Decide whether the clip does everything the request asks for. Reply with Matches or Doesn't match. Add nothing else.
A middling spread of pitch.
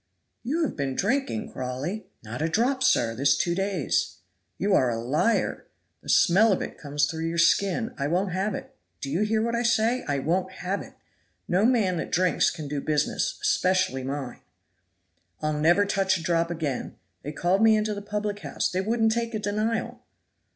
Doesn't match